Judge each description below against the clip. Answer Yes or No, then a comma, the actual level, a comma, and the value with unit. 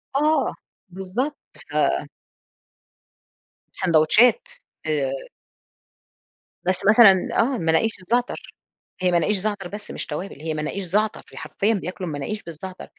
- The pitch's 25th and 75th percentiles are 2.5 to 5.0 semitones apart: Yes, average, 4.3 semitones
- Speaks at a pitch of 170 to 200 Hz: Yes, high, 190 Hz